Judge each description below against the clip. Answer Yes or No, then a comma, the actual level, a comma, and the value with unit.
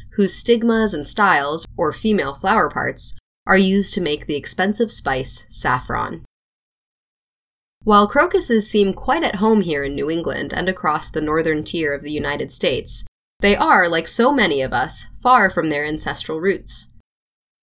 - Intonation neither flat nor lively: No, wide, 5.8 semitones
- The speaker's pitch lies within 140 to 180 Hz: No, high, 190 Hz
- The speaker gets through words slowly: No, average, 160 wpm